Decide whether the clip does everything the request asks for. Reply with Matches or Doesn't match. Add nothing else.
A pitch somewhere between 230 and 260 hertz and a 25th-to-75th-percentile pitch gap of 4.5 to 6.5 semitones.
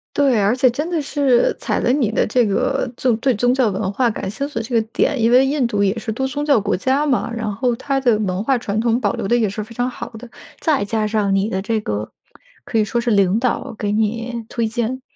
Doesn't match